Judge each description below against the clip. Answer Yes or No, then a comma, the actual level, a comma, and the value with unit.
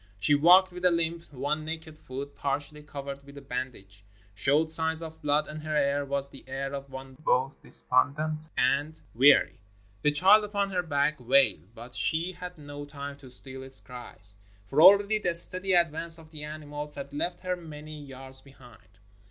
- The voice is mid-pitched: Yes, medium, 145 Hz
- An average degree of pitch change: Yes, average, 3.1 semitones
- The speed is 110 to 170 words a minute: No, average, 185 wpm